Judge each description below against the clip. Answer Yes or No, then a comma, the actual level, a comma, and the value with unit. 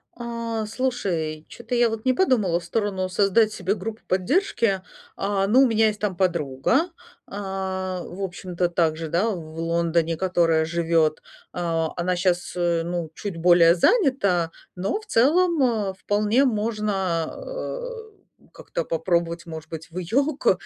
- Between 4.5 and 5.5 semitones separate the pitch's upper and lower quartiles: Yes, average, 5.0 semitones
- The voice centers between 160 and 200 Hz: Yes, high, 190 Hz